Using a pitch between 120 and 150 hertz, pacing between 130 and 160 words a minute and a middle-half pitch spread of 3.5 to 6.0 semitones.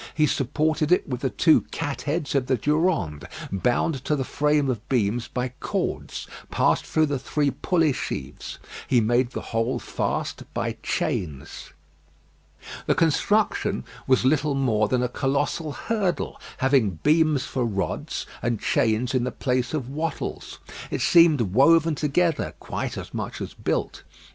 Yes: low, 135 Hz; average, 150 wpm; average, 4.1 semitones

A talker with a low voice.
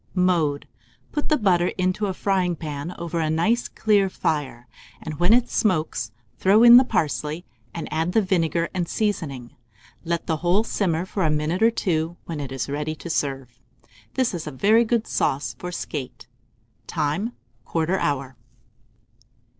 No: medium, 170 Hz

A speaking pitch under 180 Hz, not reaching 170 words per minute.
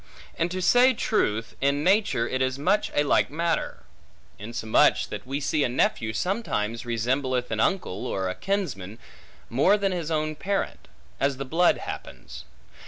Yes: medium, 140 Hz; average, 160 wpm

